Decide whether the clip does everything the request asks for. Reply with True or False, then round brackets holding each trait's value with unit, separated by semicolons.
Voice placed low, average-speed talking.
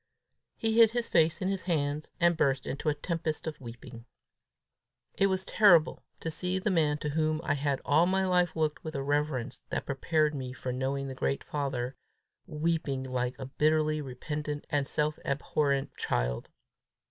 False (150 Hz; 170 wpm)